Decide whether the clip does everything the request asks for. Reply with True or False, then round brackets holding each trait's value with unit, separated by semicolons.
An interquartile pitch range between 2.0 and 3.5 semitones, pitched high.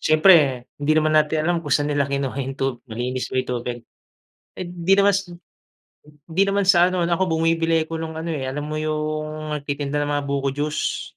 False (2.8 semitones; 155 Hz)